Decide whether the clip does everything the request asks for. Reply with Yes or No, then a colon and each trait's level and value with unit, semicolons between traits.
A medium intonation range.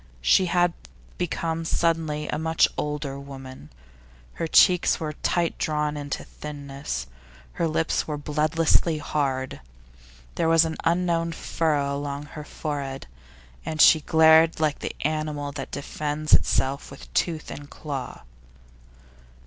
No: narrow, 2.3 semitones